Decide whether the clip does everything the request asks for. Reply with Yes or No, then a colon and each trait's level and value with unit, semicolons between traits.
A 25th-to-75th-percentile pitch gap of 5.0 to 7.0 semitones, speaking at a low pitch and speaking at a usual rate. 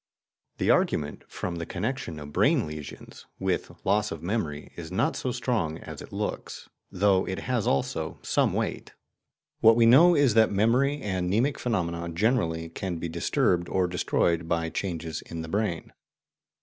Yes: wide, 5.4 semitones; very low, 95 Hz; average, 160 wpm